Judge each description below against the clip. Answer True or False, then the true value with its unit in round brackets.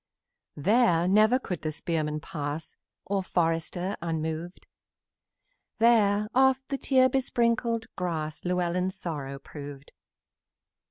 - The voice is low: False (180 Hz)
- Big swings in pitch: True (6.3 semitones)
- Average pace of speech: False (100 wpm)